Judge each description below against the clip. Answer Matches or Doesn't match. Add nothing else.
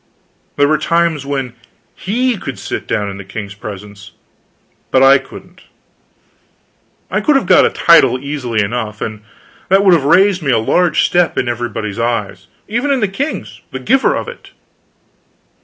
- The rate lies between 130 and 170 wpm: Matches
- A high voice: Doesn't match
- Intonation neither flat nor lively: Doesn't match